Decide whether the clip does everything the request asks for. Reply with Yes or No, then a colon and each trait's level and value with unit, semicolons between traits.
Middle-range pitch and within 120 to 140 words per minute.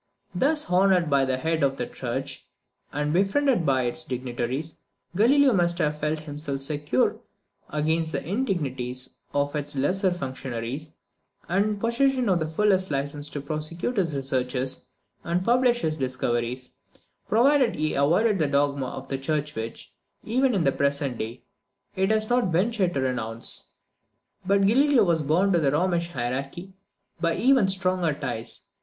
No: medium, 155 Hz; average, 155 wpm